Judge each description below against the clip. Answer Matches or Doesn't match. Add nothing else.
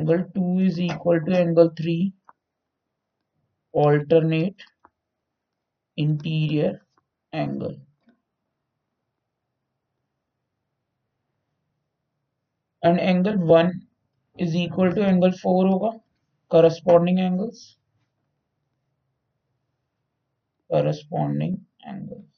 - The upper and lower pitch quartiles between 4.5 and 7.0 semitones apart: Matches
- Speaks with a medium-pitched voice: Matches